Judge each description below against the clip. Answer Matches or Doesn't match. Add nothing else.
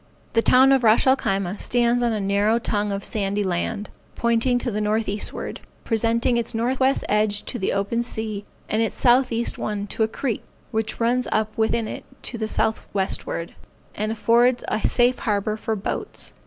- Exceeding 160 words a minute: Matches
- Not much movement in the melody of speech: Matches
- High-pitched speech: Matches